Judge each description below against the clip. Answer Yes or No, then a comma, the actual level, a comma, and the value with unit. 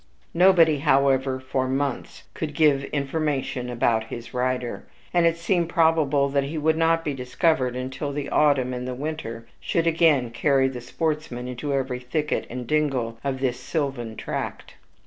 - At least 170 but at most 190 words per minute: No, average, 160 wpm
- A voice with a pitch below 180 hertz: Yes, medium, 140 Hz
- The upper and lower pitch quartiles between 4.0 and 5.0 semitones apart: No, average, 3.6 semitones